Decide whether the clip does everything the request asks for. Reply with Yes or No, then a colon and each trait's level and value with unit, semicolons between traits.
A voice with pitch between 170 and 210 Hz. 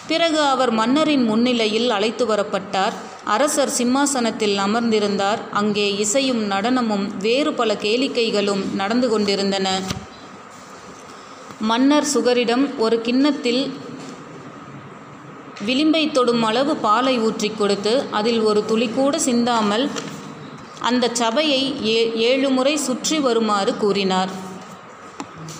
No: high, 235 Hz